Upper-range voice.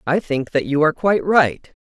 No: medium, 160 Hz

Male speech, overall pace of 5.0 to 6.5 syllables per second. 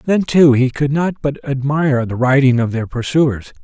No: male; 4.6 syllables/s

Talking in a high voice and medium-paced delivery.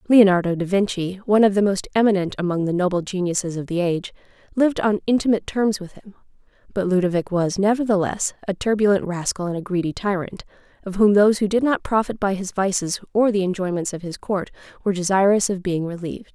Yes: high, 195 Hz; average, 195 wpm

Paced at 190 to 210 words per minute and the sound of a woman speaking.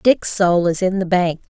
No: fast, 225 wpm; female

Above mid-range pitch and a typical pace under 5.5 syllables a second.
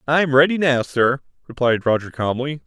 No: low, 135 Hz; 5.0 syllables/s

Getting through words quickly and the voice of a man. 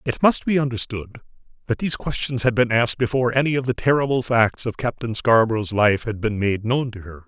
Yes: fast, 215 wpm; male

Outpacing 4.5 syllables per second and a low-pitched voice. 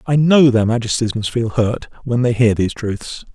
Yes: 5.1 syllables/s; low, 120 Hz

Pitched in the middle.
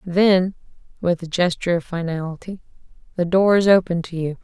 Yes: medium, 175 Hz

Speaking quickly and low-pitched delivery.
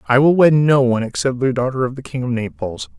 Yes: fast, 260 wpm; low, 130 Hz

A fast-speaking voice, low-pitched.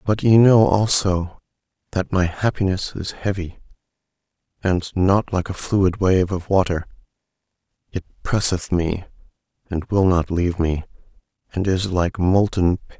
No: average, 140 wpm; very low, 95 Hz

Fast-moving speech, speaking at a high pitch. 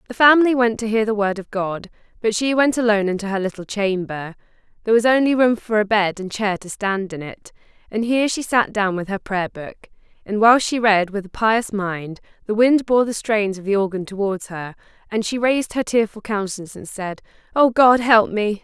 Yes: fast, 220 wpm; high, 215 Hz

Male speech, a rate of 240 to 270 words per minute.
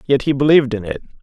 Yes: male; fast, 245 wpm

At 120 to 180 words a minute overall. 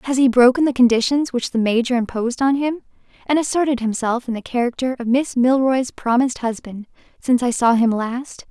No: average, 190 wpm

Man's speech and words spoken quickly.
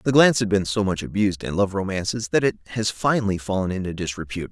Yes: male; fast, 225 wpm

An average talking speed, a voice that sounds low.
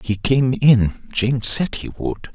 Yes: average, 180 wpm; low, 125 Hz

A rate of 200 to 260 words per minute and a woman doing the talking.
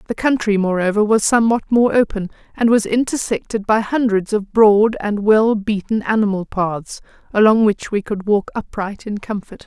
No: average, 170 wpm; female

